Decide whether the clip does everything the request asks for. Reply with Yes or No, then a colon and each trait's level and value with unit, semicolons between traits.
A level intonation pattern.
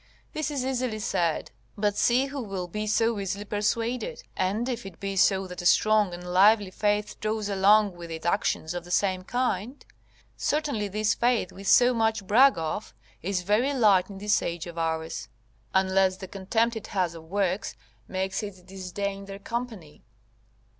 No: average, 3.2 semitones